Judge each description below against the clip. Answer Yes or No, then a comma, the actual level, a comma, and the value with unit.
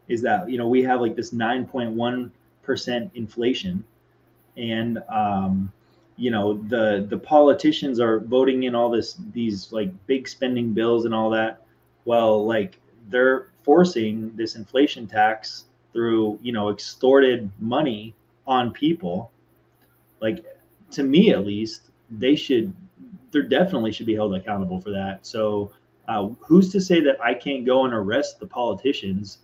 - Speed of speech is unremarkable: Yes, average, 155 wpm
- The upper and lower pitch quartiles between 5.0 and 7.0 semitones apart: No, average, 2.9 semitones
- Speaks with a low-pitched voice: Yes, low, 115 Hz